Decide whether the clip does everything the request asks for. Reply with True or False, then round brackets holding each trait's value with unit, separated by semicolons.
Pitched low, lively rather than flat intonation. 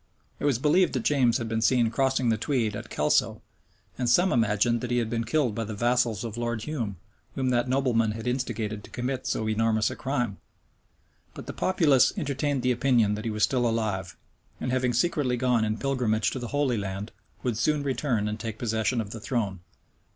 False (120 Hz; 2.9 semitones)